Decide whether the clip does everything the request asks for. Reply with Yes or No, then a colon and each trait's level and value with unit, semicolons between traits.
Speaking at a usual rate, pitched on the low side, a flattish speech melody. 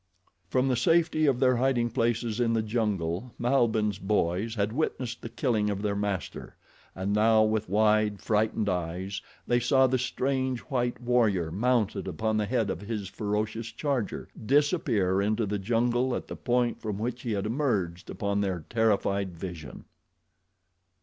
No: average, 155 wpm; low, 110 Hz; average, 3.3 semitones